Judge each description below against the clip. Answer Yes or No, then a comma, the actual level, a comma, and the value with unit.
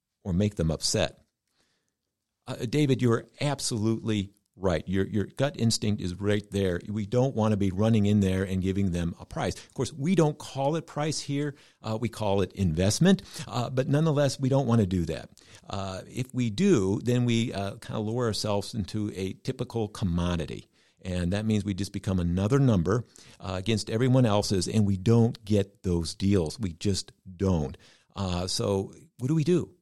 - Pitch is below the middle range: Yes, low, 105 Hz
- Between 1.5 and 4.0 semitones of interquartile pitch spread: No, average, 4.4 semitones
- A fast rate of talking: No, average, 190 wpm